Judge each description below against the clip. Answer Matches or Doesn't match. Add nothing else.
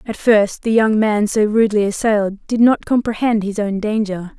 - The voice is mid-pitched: Doesn't match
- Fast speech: Doesn't match